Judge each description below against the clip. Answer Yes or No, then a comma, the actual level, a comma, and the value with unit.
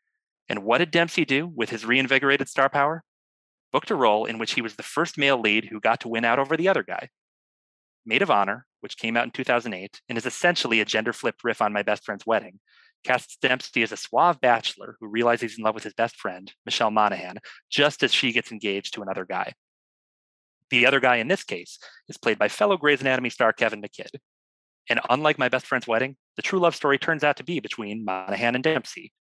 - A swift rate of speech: Yes, fast, 220 wpm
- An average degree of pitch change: No, wide, 6.1 semitones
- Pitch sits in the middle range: No, low, 130 Hz